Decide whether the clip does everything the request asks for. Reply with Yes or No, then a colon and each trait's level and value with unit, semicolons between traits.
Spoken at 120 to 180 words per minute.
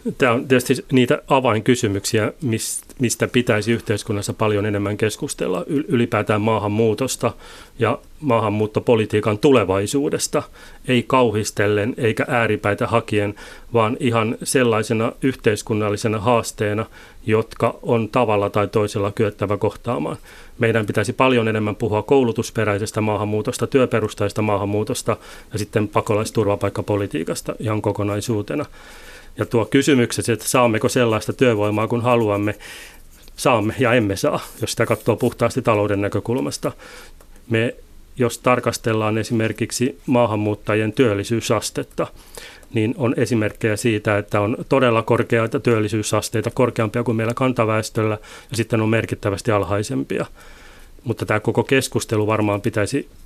No: average, 110 wpm